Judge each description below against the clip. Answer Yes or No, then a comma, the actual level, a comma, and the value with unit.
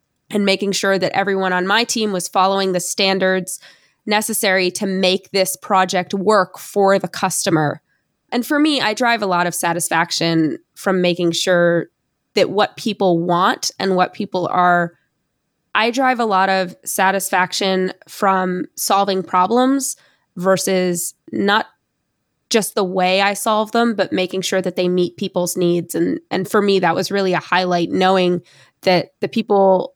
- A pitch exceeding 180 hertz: Yes, high, 190 Hz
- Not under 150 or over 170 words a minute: Yes, average, 160 wpm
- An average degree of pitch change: No, narrow, 2.1 semitones